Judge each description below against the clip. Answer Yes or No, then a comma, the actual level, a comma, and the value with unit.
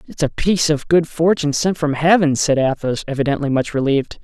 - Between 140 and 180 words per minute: No, average, 200 wpm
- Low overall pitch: No, medium, 150 Hz